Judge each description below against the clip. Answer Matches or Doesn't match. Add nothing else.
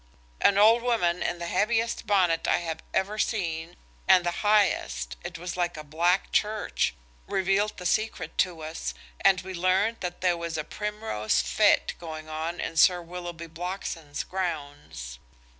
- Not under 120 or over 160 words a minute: Matches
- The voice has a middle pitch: Matches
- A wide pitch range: Doesn't match